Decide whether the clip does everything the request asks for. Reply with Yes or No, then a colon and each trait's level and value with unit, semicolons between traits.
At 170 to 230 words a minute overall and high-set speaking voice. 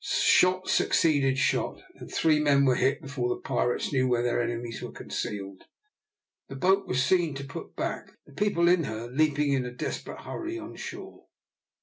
No: average, 180 wpm; medium, 140 Hz